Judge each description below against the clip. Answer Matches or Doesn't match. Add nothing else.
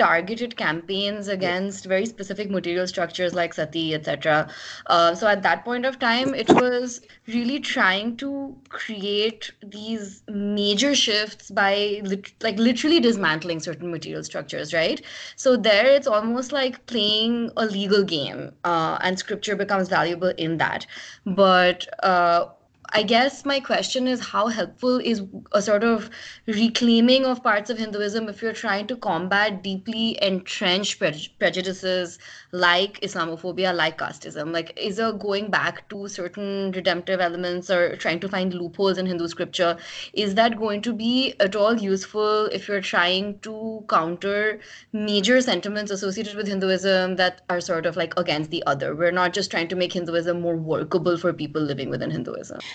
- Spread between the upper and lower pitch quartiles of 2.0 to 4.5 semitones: Matches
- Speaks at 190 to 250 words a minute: Doesn't match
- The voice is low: Doesn't match